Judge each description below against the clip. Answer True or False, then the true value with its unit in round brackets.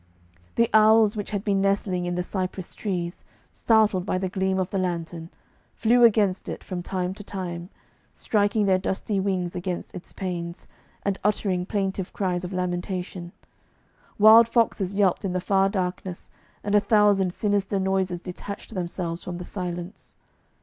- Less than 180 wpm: True (155 wpm)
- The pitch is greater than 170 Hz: True (190 Hz)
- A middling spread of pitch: False (2.3 semitones)